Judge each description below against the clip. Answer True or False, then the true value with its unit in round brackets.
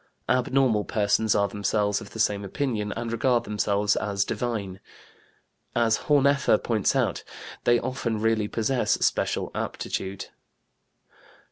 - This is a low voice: True (110 Hz)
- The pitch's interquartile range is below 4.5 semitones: True (2.7 semitones)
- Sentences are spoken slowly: True (120 wpm)